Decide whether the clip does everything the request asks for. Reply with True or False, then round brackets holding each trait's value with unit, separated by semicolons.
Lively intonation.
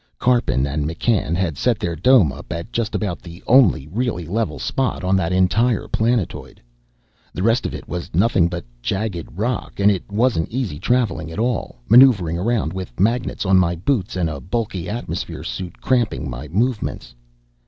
True (5.7 semitones)